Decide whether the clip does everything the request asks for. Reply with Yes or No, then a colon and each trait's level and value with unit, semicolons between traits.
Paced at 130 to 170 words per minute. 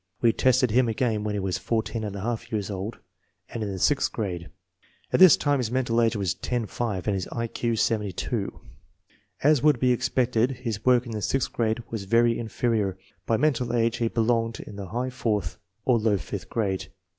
No: average, 195 wpm